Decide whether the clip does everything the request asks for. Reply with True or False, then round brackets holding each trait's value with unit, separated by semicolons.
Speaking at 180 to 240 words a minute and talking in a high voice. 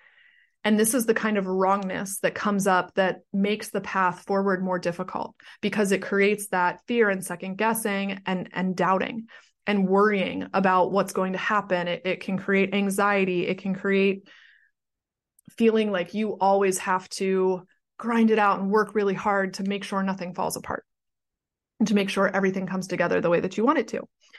True (185 wpm; 195 Hz)